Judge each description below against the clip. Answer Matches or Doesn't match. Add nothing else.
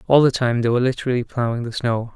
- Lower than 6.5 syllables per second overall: Doesn't match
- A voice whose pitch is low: Matches